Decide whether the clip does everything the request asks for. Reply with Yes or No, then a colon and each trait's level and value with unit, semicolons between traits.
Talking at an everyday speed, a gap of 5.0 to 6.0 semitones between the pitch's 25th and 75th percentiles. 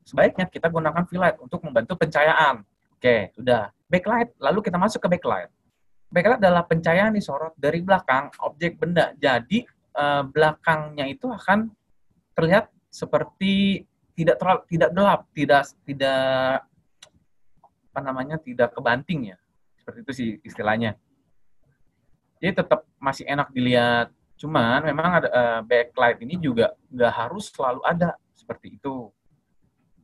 Yes: average, 130 wpm; wide, 5.5 semitones